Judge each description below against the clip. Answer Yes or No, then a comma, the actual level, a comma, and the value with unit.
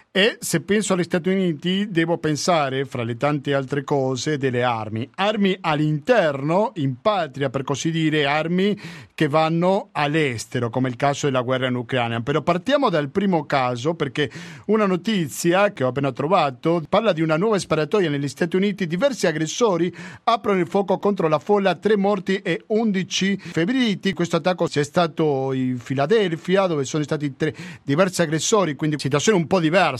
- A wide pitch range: No, average, 4.9 semitones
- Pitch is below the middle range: No, medium, 165 Hz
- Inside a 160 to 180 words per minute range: Yes, fast, 170 wpm